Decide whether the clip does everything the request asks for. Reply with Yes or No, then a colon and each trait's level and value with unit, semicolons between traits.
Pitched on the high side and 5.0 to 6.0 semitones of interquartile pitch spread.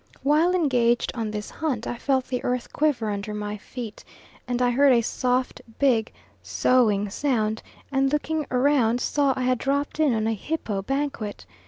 No: very high, 250 Hz; average, 4.1 semitones